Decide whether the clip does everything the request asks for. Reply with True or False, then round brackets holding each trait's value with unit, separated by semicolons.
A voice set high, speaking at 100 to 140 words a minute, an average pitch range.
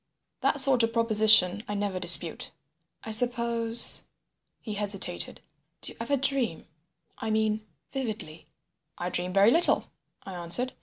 True (220 Hz; 135 wpm; 3.2 semitones)